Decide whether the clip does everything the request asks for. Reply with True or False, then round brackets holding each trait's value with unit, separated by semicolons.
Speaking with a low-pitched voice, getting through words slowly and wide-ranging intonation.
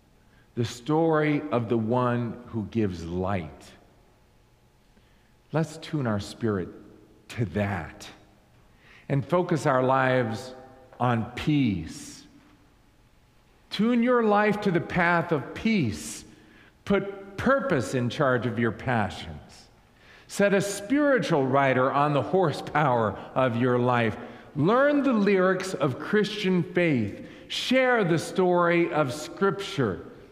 True (130 Hz; 110 wpm; 7.8 semitones)